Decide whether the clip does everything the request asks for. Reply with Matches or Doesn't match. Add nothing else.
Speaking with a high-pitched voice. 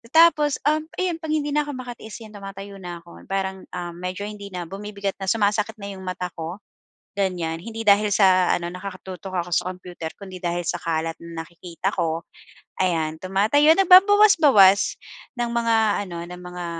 Matches